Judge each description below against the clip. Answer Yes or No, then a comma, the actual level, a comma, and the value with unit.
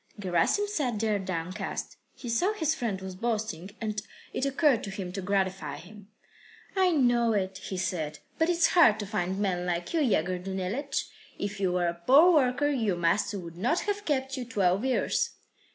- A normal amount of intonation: No, wide, 6.2 semitones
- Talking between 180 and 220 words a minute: Yes, average, 185 wpm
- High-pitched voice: Yes, high, 210 Hz